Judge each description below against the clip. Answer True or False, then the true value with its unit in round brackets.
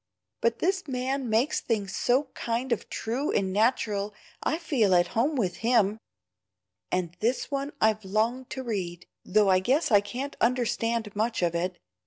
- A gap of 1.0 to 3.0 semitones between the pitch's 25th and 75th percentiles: False (4.3 semitones)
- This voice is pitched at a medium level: False (230 Hz)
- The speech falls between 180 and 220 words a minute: False (165 wpm)